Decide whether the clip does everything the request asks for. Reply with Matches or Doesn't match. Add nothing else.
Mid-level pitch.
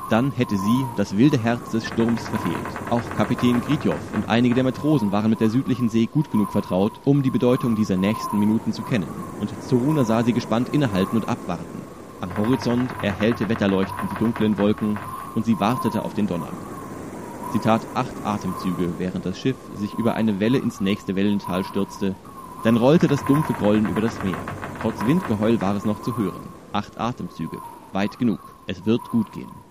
Doesn't match